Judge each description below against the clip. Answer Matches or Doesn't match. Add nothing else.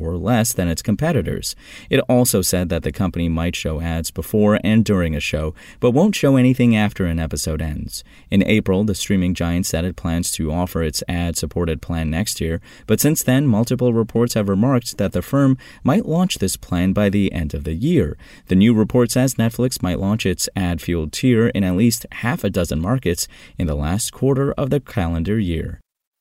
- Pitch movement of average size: Doesn't match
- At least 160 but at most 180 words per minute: Doesn't match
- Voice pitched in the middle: Doesn't match